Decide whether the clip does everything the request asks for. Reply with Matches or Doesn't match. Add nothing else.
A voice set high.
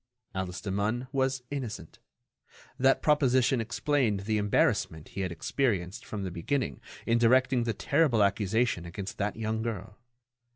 Doesn't match